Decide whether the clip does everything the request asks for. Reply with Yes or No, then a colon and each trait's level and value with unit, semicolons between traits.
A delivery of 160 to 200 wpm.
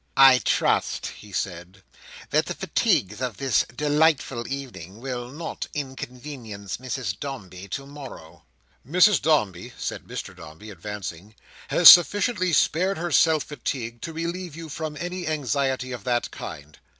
No: slow, 135 wpm